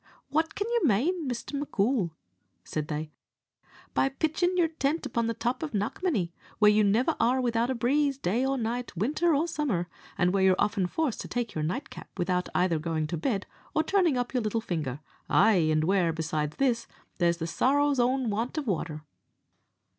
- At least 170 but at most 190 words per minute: Yes, average, 185 wpm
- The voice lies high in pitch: Yes, high, 230 Hz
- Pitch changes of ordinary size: No, wide, 7.5 semitones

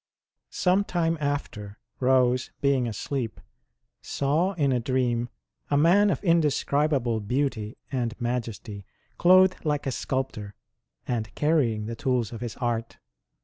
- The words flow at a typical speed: No, slow, 125 wpm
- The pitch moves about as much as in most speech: Yes, average, 4.2 semitones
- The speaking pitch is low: Yes, low, 130 Hz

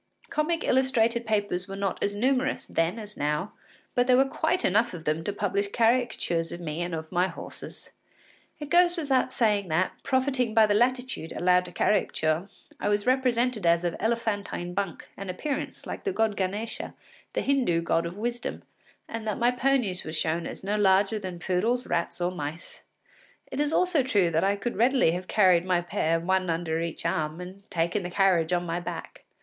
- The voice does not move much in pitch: No, wide, 5.6 semitones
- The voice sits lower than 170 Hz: No, high, 200 Hz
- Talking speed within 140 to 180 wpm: No, average, 190 wpm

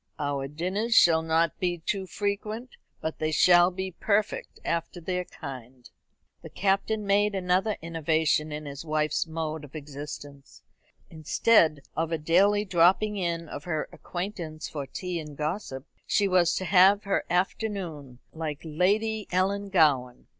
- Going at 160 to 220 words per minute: No, average, 140 wpm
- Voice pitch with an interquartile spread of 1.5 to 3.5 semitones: No, average, 4.2 semitones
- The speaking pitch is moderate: Yes, medium, 170 Hz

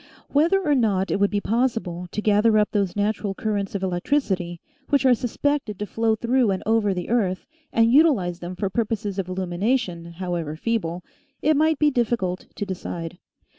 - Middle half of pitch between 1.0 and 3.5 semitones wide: No, average, 4.6 semitones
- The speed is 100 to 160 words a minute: No, average, 175 wpm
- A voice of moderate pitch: No, high, 205 Hz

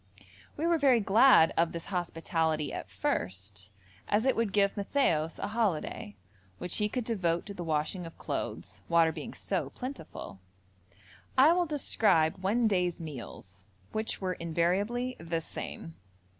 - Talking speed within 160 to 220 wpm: No, average, 145 wpm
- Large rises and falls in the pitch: Yes, wide, 5.7 semitones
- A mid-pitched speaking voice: Yes, medium, 180 Hz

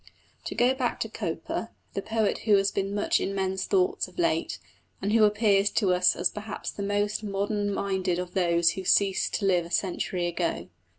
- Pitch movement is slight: Yes, narrow, 2.3 semitones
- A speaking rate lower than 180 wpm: No, average, 195 wpm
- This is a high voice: Yes, high, 200 Hz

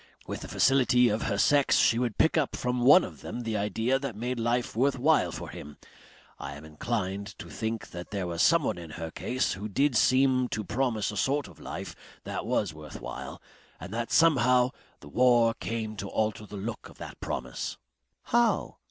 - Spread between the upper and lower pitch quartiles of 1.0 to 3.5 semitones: No, average, 4.0 semitones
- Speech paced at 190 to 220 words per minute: Yes, average, 195 wpm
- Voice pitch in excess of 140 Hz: No, low, 115 Hz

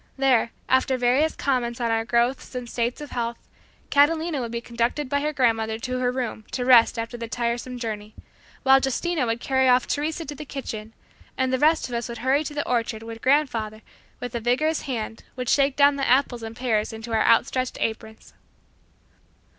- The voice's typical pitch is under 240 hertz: No, very high, 250 Hz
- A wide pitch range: No, average, 2.8 semitones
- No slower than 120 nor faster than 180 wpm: No, average, 195 wpm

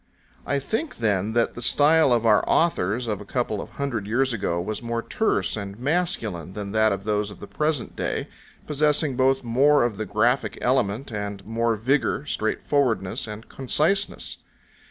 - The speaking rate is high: No, average, 170 wpm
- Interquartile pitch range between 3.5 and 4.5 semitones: No, average, 4.9 semitones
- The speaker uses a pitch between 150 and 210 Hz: No, low, 115 Hz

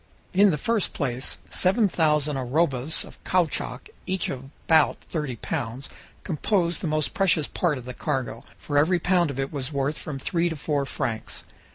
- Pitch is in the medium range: Yes, medium, 150 Hz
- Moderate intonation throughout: Yes, average, 4.3 semitones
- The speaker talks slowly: No, average, 175 wpm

